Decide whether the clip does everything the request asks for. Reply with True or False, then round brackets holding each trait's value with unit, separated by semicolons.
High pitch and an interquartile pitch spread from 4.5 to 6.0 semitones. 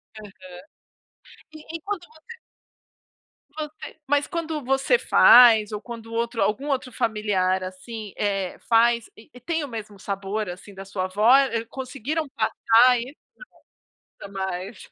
True (230 Hz; 5.0 semitones)